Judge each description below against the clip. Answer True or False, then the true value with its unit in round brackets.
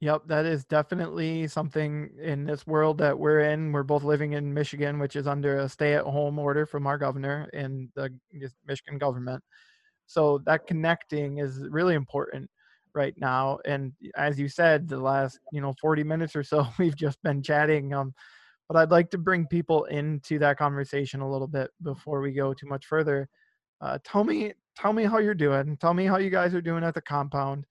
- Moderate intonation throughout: False (2.3 semitones)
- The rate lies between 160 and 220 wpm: True (200 wpm)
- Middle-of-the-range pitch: True (145 Hz)